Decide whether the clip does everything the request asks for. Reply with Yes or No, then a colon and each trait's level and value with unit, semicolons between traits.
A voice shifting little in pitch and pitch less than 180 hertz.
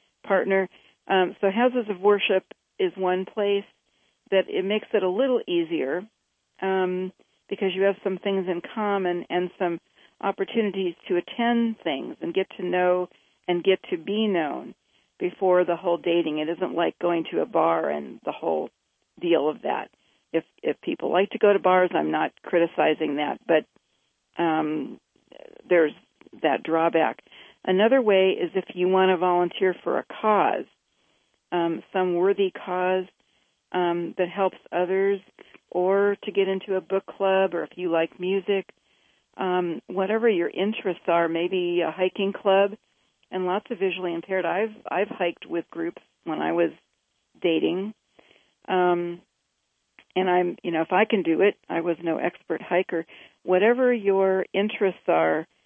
No: narrow, 2.3 semitones; medium, 185 Hz